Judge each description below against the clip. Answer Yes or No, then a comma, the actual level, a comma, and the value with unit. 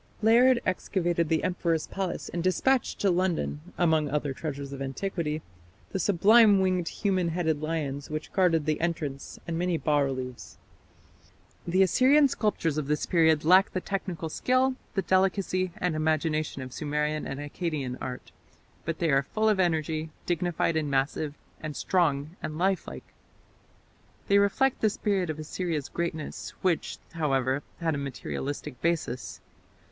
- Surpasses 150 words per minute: No, average, 145 wpm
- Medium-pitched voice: Yes, medium, 165 Hz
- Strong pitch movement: No, average, 3.7 semitones